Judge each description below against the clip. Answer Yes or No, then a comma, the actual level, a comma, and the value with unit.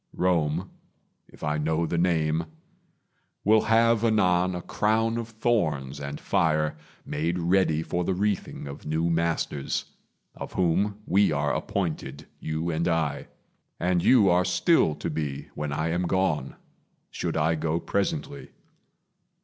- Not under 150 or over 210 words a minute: No, average, 140 wpm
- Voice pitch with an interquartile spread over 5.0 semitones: No, average, 4.0 semitones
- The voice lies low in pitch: Yes, very low, 85 Hz